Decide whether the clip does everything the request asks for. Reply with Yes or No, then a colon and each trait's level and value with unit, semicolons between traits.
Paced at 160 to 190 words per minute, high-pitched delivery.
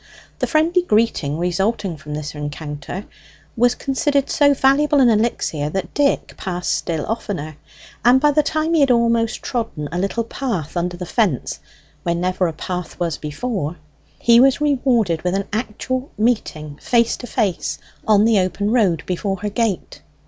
Yes: average, 165 wpm; high, 210 Hz